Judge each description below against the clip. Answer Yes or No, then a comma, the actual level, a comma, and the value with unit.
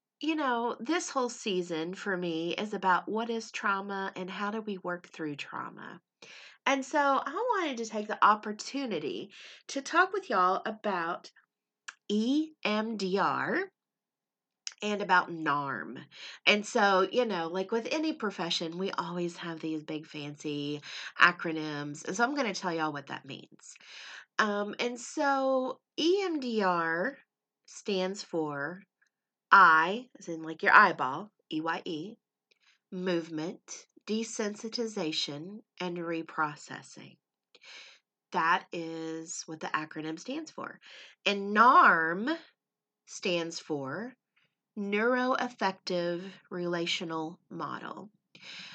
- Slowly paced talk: Yes, slow, 110 wpm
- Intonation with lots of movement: Yes, wide, 6.3 semitones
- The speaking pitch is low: No, high, 195 Hz